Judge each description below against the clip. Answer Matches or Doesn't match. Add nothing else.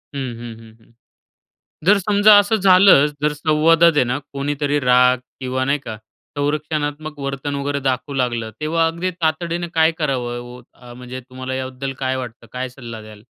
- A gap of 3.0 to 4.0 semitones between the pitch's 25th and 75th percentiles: Matches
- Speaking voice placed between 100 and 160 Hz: Matches